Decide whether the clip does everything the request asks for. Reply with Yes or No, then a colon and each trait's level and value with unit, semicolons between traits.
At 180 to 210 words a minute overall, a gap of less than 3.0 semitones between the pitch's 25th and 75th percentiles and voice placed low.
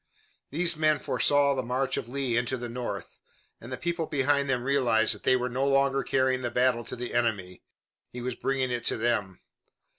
Yes: average, 200 wpm; narrow, 2.4 semitones; low, 130 Hz